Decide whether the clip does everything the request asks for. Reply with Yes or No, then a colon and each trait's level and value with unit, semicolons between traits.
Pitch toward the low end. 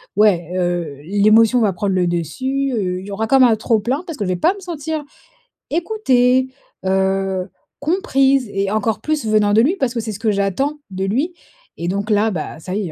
No: high, 215 Hz